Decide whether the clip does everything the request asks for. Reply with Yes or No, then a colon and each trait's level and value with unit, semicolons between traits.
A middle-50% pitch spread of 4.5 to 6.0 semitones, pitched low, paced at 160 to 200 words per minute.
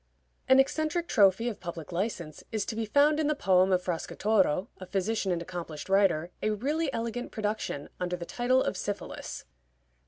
No: average, 5.2 semitones; high, 205 Hz; average, 175 wpm